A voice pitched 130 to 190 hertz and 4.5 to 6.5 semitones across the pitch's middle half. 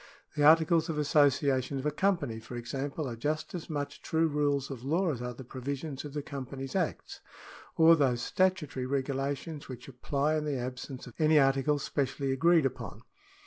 No: medium, 140 Hz; average, 2.7 semitones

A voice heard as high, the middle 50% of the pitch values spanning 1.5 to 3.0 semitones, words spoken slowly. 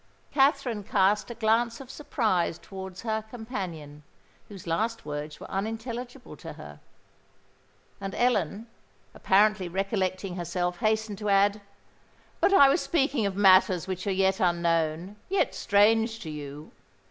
No: high, 200 Hz; average, 3.7 semitones; slow, 130 wpm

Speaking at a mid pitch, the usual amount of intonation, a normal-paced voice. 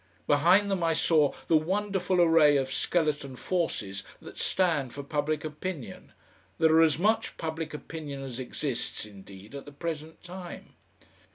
Yes: medium, 155 Hz; average, 3.6 semitones; average, 150 wpm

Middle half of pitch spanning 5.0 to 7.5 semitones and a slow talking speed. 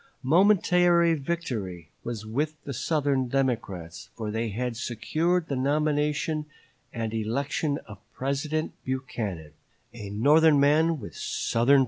Yes: wide, 5.5 semitones; slow, 120 wpm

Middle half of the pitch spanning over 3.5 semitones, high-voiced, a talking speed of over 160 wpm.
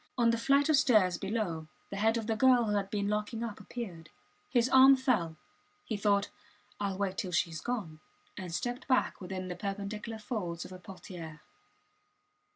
Yes: average, 4.2 semitones; high, 205 Hz; average, 180 wpm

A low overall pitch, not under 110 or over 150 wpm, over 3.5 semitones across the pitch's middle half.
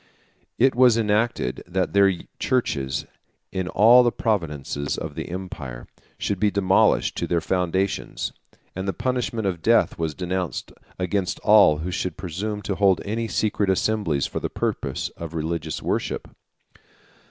Yes: very low, 95 Hz; average, 145 wpm; average, 4.1 semitones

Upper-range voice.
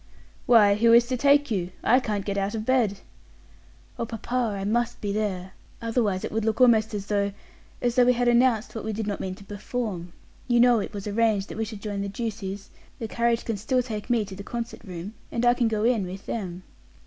Yes: high, 220 Hz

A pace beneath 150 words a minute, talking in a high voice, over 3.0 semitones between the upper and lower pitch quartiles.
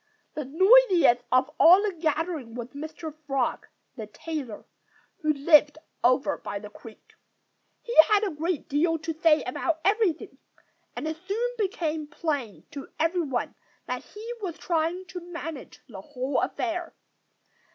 Yes: average, 140 wpm; very high, 315 Hz; average, 4.2 semitones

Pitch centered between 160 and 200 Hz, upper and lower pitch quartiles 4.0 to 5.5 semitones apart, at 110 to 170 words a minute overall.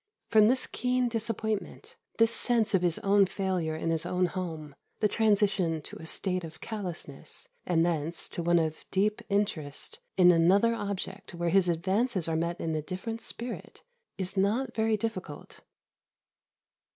Yes: high, 190 Hz; average, 4.5 semitones; average, 155 wpm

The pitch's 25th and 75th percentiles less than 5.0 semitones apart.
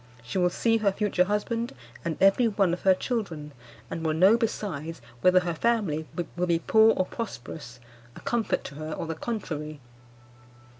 No: average, 5.3 semitones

